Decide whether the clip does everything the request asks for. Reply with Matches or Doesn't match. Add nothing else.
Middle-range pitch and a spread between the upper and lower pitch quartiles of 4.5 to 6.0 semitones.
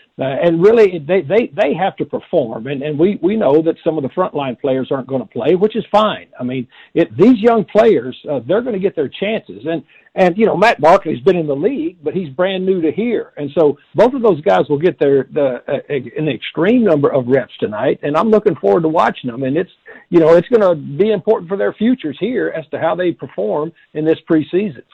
Matches